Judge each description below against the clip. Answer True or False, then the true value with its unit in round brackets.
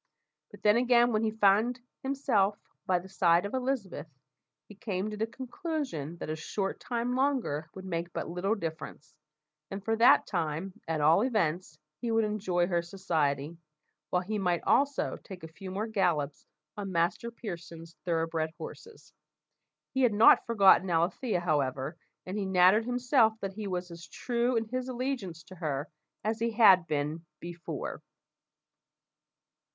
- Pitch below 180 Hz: False (190 Hz)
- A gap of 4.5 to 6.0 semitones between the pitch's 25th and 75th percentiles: True (5.2 semitones)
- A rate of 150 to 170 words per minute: True (155 wpm)